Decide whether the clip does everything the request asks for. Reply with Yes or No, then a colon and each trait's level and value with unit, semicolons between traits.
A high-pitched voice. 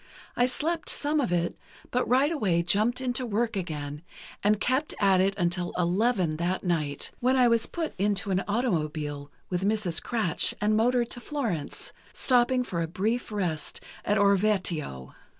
Yes: high, 205 Hz